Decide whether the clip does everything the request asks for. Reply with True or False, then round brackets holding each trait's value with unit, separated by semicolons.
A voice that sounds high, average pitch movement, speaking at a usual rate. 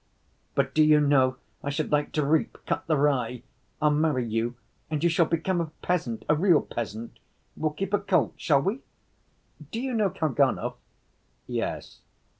False (150 Hz; 3.7 semitones; 170 wpm)